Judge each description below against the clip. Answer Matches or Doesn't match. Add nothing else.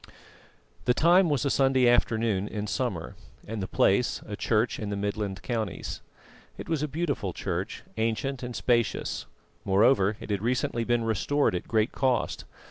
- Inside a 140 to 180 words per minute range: Matches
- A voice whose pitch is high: Doesn't match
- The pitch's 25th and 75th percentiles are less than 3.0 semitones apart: Doesn't match